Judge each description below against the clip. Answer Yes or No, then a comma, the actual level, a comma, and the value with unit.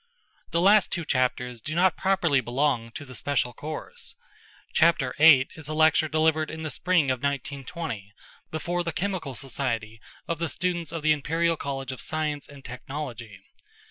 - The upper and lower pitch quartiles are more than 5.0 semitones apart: No, average, 4.2 semitones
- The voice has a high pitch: No, medium, 150 Hz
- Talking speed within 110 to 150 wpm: No, average, 165 wpm